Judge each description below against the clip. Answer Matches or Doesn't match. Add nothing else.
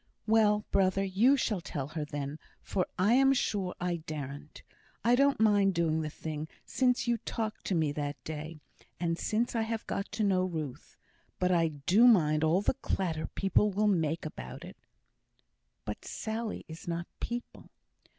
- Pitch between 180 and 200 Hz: Matches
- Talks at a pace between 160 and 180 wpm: Matches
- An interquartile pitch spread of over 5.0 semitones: Matches